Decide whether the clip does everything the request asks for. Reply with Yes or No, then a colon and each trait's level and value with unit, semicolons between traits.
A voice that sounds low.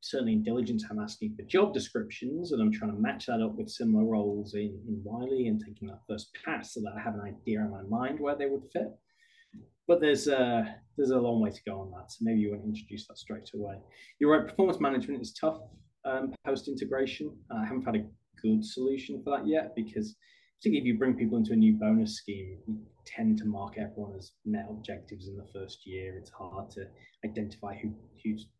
Yes: low, 115 Hz